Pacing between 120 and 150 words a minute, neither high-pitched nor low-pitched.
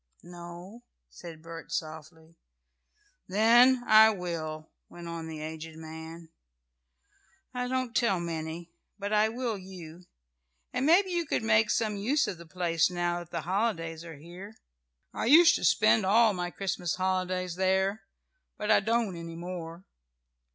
Yes: average, 145 wpm; medium, 180 Hz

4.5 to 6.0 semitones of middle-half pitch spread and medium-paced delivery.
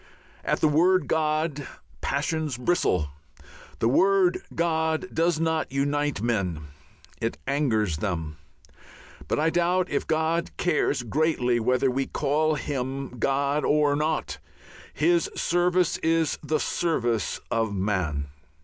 No: average, 5.1 semitones; slow, 120 wpm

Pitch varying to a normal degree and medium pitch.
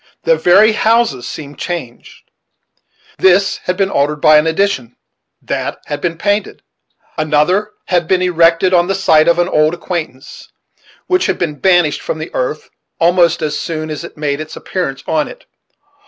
Yes: average, 3.5 semitones; medium, 170 Hz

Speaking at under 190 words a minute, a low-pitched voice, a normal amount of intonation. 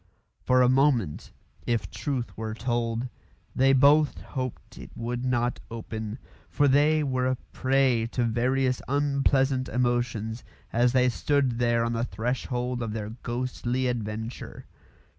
No: slow, 135 wpm; low, 125 Hz; narrow, 2.1 semitones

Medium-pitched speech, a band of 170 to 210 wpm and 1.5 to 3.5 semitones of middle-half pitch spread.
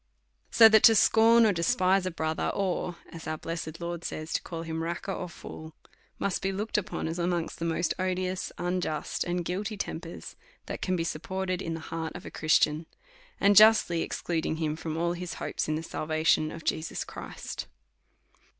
Yes: medium, 170 Hz; average, 185 wpm; narrow, 2.4 semitones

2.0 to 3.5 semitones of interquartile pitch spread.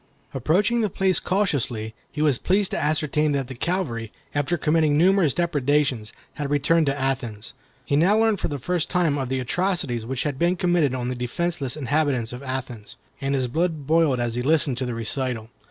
No: average, 4.9 semitones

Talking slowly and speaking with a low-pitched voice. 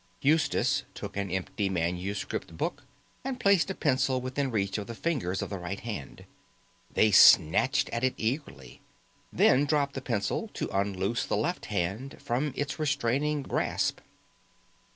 No: average, 150 wpm; low, 120 Hz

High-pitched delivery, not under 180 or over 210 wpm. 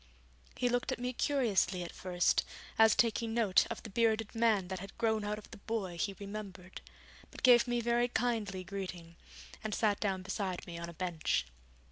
Yes: high, 205 Hz; average, 185 wpm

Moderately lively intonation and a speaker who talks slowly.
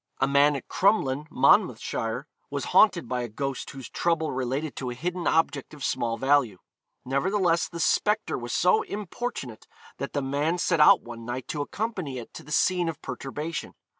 No: average, 4.6 semitones; average, 175 wpm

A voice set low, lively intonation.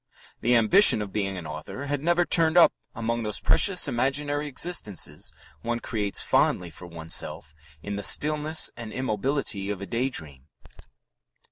Yes: low, 115 Hz; wide, 6.6 semitones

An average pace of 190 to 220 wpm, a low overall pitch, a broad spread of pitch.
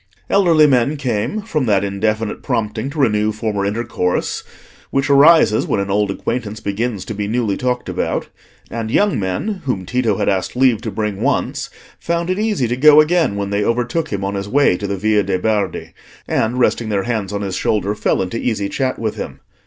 No: average, 200 wpm; low, 110 Hz; average, 4.7 semitones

